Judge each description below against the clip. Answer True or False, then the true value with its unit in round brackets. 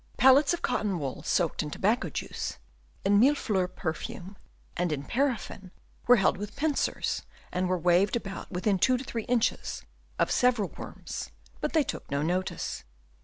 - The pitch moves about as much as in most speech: False (5.7 semitones)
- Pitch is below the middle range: False (200 Hz)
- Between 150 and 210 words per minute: True (160 wpm)